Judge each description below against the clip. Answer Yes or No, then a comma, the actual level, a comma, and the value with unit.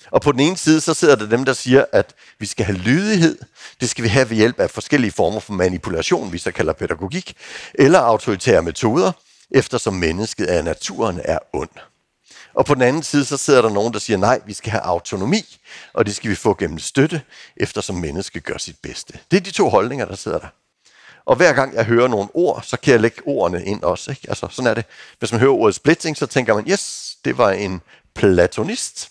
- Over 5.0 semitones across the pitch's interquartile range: Yes, wide, 5.4 semitones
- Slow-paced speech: No, fast, 225 wpm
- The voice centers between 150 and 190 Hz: No, low, 125 Hz